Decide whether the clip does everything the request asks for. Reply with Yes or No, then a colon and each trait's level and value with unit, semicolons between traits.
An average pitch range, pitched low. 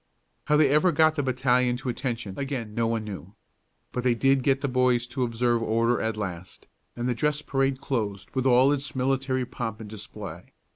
Yes: average, 3.1 semitones; low, 125 Hz